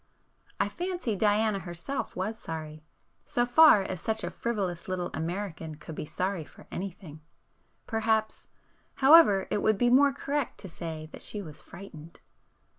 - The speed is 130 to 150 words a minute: Yes, average, 145 wpm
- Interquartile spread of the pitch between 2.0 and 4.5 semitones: No, average, 5.0 semitones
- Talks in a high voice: Yes, high, 195 Hz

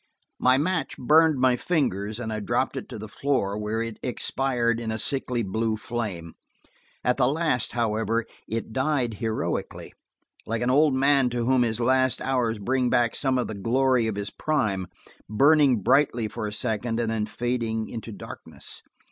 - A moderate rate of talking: Yes, average, 170 wpm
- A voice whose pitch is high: No, low, 120 Hz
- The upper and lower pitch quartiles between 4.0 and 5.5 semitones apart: No, average, 3.1 semitones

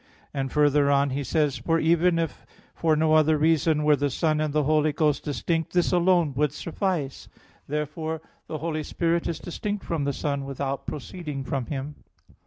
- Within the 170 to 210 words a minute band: Yes, average, 180 wpm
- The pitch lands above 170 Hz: No, medium, 150 Hz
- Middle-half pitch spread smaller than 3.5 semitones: Yes, narrow, 2.5 semitones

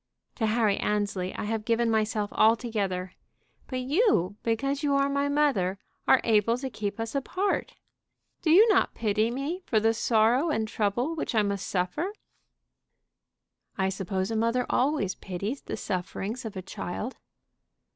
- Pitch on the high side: Yes, high, 225 Hz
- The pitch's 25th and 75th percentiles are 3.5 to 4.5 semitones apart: No, average, 5.0 semitones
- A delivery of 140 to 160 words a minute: Yes, average, 155 wpm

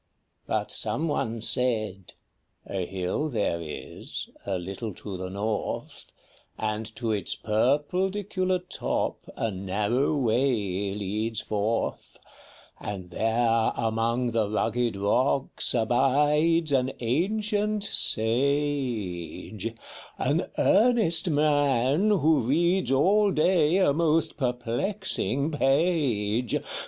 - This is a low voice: Yes, low, 125 Hz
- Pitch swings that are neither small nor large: No, wide, 6.3 semitones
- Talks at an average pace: No, slow, 105 wpm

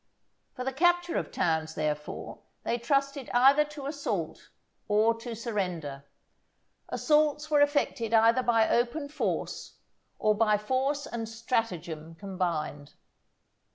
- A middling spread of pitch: No, wide, 7.1 semitones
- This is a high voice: Yes, high, 230 Hz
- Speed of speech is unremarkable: No, slow, 120 wpm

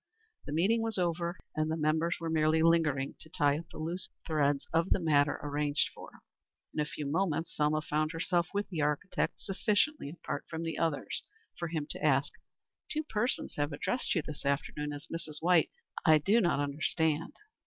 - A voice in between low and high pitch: Yes, medium, 160 Hz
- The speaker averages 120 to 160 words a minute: No, average, 185 wpm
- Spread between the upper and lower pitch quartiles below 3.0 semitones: Yes, narrow, 2.6 semitones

